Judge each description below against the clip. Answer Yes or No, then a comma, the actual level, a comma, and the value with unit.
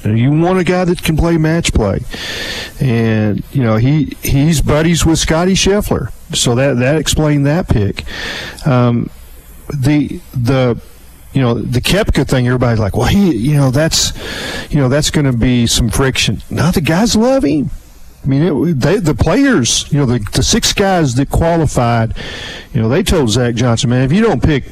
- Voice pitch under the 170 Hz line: Yes, low, 135 Hz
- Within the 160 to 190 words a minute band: Yes, average, 185 wpm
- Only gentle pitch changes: No, average, 5.2 semitones